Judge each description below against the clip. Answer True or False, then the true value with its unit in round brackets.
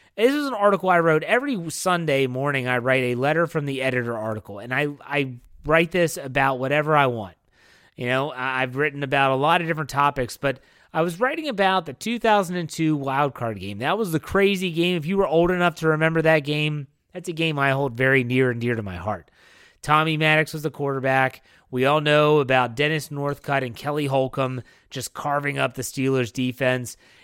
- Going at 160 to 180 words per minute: False (205 wpm)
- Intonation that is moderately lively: True (3.7 semitones)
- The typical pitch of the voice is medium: True (145 Hz)